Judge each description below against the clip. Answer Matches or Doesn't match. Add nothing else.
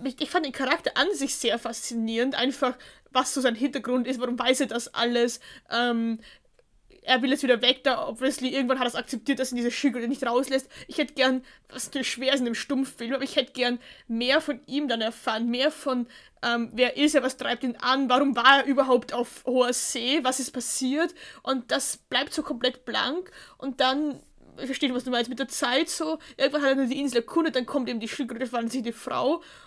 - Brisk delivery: Matches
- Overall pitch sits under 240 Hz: Doesn't match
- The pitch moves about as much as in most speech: Doesn't match